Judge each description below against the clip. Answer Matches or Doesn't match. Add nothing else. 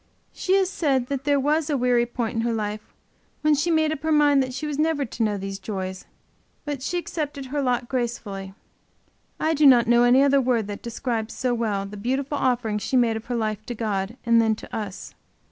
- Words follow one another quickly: Matches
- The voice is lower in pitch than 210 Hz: Doesn't match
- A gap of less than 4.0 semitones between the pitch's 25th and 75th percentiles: Doesn't match